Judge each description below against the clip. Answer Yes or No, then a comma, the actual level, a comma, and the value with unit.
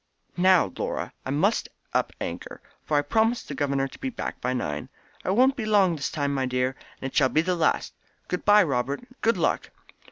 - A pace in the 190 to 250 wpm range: Yes, average, 200 wpm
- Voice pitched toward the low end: No, medium, 165 Hz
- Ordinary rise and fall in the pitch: No, wide, 7.2 semitones